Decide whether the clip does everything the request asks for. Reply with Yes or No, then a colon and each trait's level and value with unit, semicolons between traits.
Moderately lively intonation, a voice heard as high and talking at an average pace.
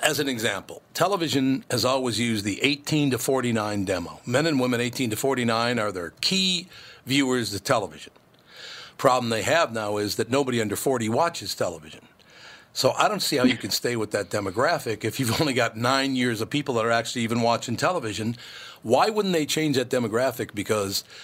No: average, 3.5 semitones; low, 125 Hz; average, 190 wpm